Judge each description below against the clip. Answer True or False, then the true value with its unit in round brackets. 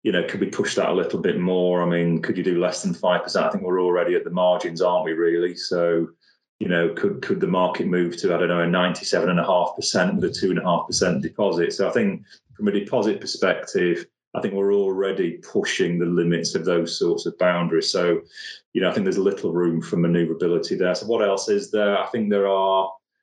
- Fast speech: True (245 wpm)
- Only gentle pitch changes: True (1.8 semitones)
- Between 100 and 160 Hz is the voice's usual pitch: False (90 Hz)